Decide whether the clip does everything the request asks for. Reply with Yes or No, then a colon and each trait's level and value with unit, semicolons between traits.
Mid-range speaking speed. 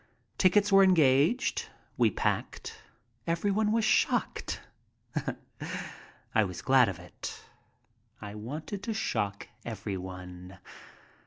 No: slow, 95 wpm